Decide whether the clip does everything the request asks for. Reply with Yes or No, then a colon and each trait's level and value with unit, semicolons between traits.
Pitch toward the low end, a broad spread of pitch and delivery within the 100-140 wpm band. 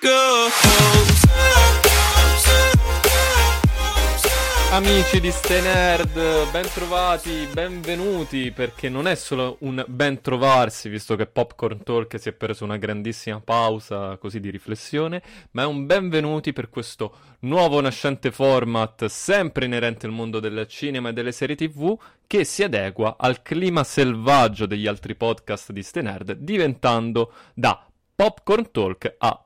Yes: low, 130 Hz; wide, 6.6 semitones; average, 120 wpm